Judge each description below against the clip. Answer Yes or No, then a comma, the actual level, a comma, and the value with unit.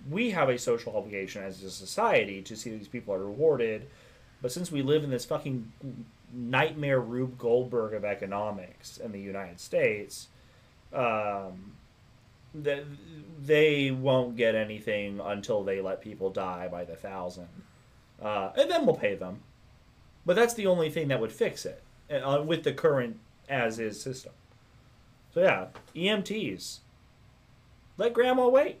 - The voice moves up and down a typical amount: No, wide, 6.6 semitones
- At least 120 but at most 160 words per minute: Yes, average, 150 wpm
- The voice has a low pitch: Yes, low, 125 Hz